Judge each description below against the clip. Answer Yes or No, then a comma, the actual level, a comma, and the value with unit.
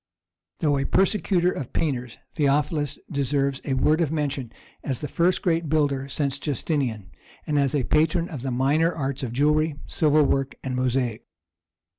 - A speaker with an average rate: Yes, average, 160 wpm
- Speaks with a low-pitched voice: No, medium, 145 Hz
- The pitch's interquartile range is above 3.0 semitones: No, narrow, 2.6 semitones